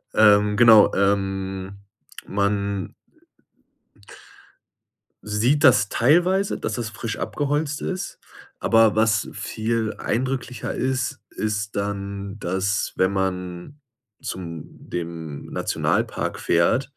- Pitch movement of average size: Yes, average, 3.6 semitones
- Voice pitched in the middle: No, low, 105 Hz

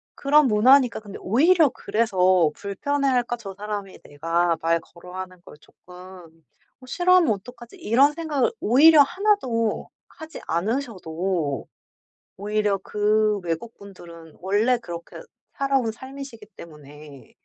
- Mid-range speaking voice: No, high, 210 Hz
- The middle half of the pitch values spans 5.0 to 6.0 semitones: No, wide, 6.8 semitones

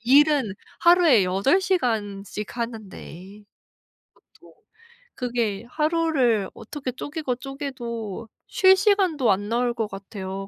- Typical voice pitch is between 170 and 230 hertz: No, high, 240 Hz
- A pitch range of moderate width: No, wide, 6.3 semitones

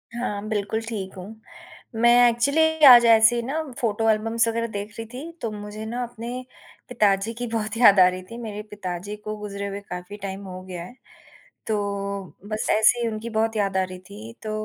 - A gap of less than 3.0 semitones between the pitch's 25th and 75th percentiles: Yes, narrow, 2.5 semitones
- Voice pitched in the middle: No, high, 215 Hz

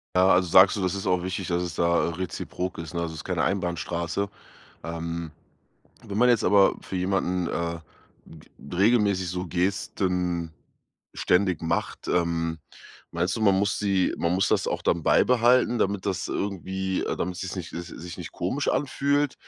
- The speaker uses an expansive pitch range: No, narrow, 2.5 semitones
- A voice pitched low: Yes, very low, 90 Hz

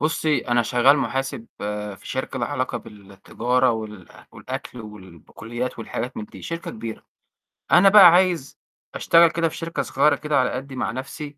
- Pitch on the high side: No, low, 130 Hz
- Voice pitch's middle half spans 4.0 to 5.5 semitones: Yes, average, 4.7 semitones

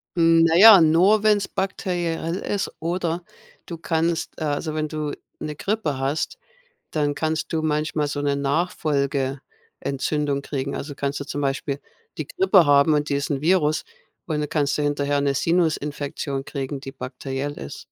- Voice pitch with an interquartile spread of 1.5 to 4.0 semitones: Yes, average, 2.8 semitones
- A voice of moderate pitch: Yes, medium, 150 Hz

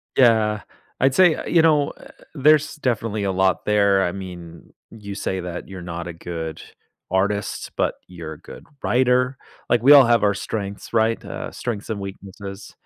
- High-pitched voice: No, low, 100 Hz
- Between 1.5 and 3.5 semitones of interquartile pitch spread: No, average, 4.5 semitones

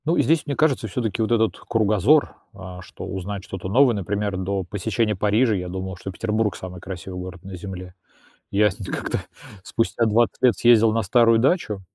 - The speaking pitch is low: Yes, low, 105 Hz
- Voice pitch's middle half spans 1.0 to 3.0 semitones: No, average, 3.4 semitones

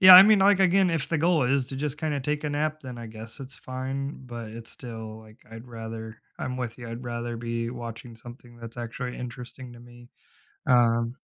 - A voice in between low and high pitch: No, low, 120 Hz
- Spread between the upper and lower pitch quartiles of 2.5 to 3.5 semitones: Yes, average, 3.1 semitones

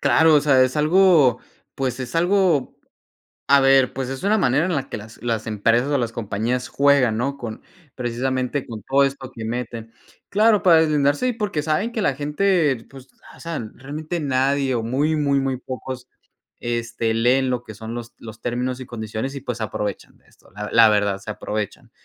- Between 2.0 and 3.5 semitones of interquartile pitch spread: No, average, 3.9 semitones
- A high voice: No, low, 130 Hz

